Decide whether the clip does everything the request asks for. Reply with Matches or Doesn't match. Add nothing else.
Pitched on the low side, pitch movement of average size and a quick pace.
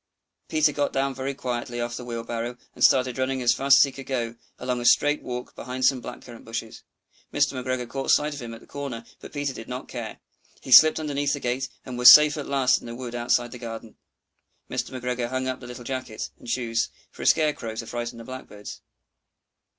Doesn't match